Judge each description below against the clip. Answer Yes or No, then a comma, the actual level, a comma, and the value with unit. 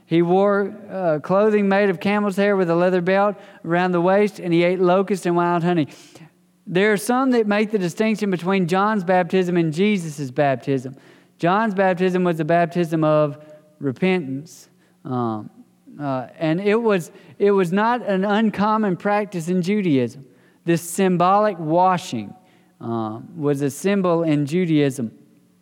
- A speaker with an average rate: Yes, average, 150 wpm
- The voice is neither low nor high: Yes, medium, 180 Hz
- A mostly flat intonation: No, average, 4.1 semitones